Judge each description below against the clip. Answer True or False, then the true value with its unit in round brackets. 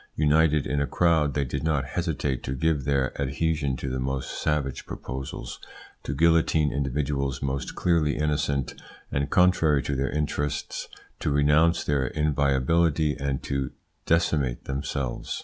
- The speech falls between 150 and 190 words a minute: False (140 wpm)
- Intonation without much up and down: True (2.2 semitones)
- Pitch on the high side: False (70 Hz)